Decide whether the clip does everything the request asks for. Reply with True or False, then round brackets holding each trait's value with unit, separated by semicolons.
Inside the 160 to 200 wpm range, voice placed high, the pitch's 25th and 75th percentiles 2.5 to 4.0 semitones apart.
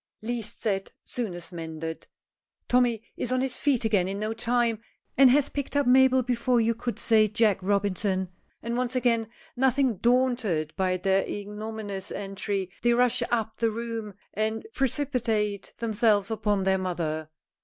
False (150 wpm; 220 Hz; 3.7 semitones)